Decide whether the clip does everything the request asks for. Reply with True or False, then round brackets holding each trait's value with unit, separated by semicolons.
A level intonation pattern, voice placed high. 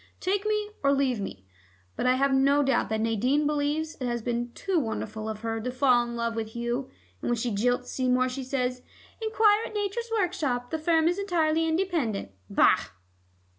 False (5.3 semitones; 265 Hz)